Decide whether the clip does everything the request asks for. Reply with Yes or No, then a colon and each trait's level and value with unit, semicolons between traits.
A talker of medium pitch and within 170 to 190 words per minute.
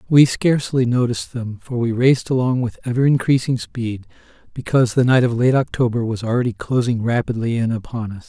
No: low, 120 Hz; average, 180 wpm